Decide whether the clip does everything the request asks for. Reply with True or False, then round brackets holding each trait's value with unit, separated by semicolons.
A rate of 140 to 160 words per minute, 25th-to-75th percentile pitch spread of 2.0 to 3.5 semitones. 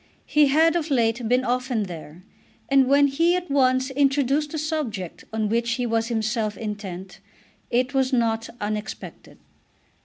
False (150 wpm; 4.1 semitones)